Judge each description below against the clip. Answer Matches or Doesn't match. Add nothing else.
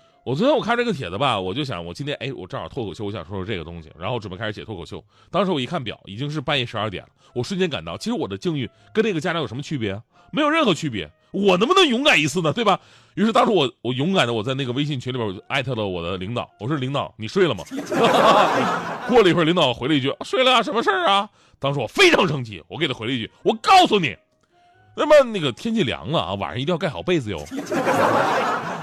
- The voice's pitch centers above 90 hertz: Matches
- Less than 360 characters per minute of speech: Doesn't match